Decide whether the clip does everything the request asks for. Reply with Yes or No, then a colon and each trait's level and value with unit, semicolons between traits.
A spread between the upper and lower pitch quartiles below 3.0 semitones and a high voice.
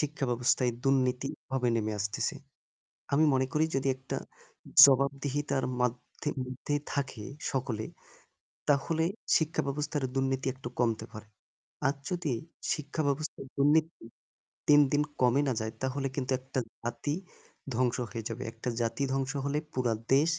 No: narrow, 2.5 semitones; low, 135 Hz